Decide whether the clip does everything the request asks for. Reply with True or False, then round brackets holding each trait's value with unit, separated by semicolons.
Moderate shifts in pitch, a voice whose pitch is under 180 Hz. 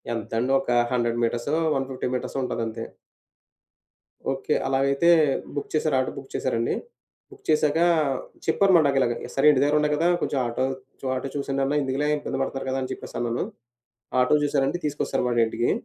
True (3.1 semitones; 135 Hz)